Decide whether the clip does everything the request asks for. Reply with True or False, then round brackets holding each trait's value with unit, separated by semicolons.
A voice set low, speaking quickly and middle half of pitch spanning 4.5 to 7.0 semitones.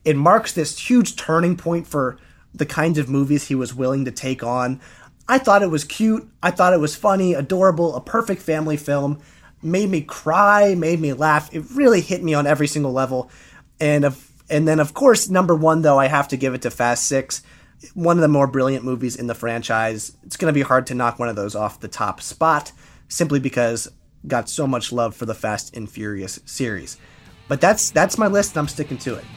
False (145 Hz; 220 wpm; 5.0 semitones)